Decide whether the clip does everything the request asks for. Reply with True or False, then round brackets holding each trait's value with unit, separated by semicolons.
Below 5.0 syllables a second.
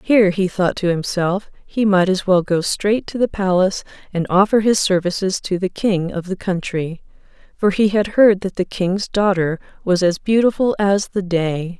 True (4.7 syllables/s)